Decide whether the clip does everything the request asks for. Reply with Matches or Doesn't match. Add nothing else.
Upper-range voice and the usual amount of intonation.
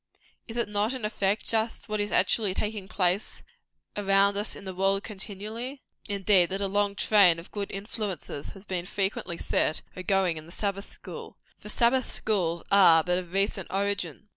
Doesn't match